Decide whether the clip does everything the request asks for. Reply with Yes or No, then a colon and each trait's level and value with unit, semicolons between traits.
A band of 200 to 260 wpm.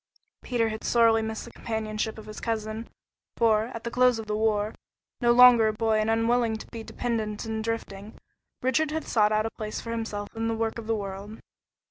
Yes: fast, 205 wpm